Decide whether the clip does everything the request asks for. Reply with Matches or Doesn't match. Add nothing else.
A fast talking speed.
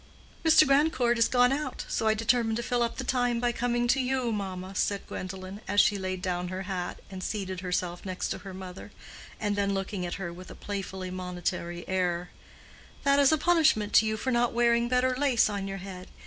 Matches